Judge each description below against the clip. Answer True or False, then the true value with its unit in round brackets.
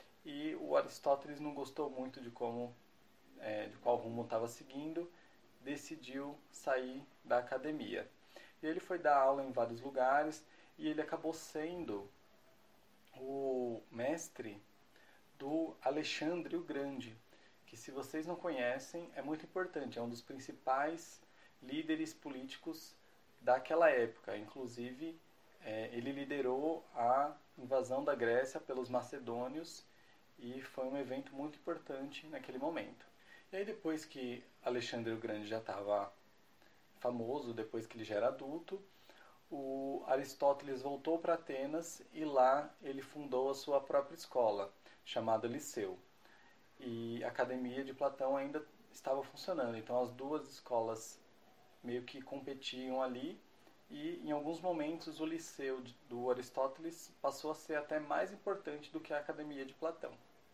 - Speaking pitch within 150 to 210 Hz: False (140 Hz)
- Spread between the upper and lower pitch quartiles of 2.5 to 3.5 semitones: False (4.0 semitones)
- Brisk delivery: False (135 wpm)